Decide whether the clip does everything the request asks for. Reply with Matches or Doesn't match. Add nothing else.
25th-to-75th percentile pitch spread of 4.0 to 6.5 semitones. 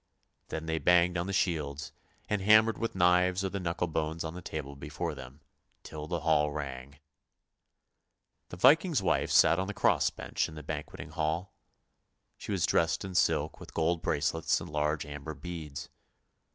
Doesn't match